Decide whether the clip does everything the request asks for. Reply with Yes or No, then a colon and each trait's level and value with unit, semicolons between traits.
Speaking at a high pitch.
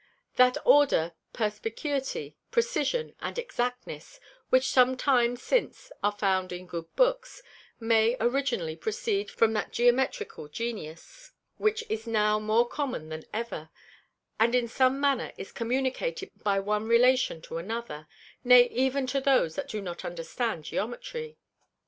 Yes: high, 240 Hz